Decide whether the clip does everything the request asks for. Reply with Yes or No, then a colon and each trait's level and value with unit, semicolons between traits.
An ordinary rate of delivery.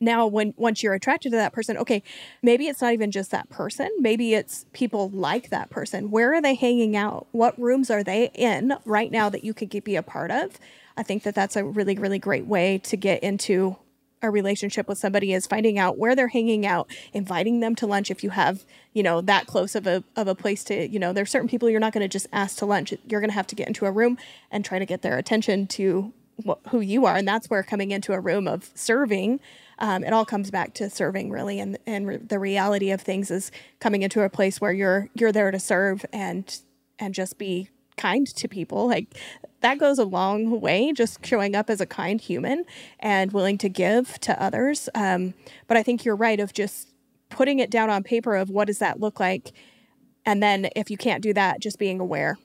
No: fast, 235 wpm